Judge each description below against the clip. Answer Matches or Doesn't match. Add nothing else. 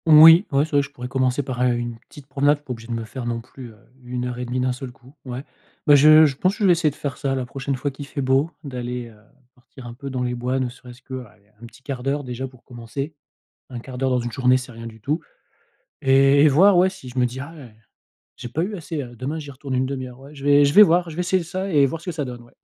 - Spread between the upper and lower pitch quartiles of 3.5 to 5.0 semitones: Doesn't match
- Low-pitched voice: Matches